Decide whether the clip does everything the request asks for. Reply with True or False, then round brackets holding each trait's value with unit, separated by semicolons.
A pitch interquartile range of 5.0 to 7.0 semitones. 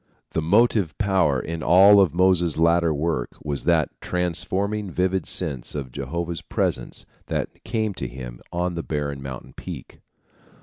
False (4.4 semitones)